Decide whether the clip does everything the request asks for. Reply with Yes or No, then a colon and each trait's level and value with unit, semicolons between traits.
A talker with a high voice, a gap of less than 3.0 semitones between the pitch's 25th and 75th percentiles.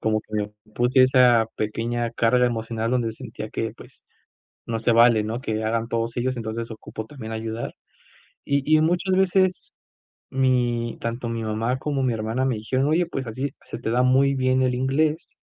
No: low, 120 Hz; narrow, 2.6 semitones